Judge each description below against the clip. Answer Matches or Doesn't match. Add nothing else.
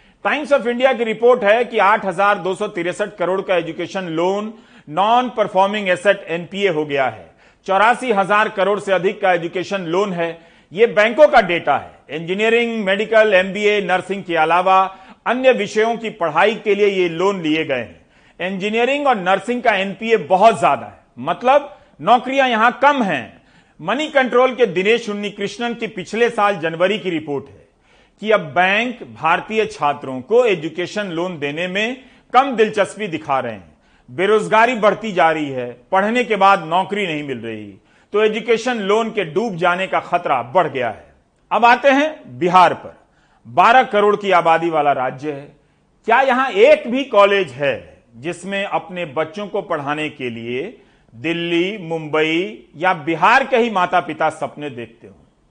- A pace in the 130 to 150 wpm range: Doesn't match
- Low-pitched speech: Doesn't match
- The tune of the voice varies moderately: Matches